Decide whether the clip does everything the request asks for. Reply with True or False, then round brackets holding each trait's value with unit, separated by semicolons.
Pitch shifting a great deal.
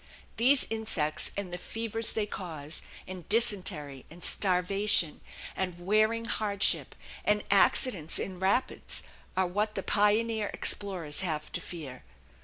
False (3.6 semitones)